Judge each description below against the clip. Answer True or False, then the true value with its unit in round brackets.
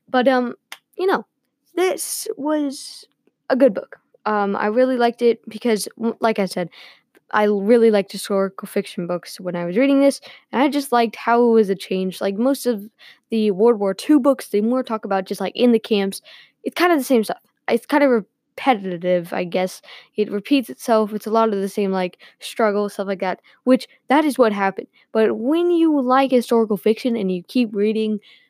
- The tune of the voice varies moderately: True (4.3 semitones)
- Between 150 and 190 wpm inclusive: False (200 wpm)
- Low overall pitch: False (225 Hz)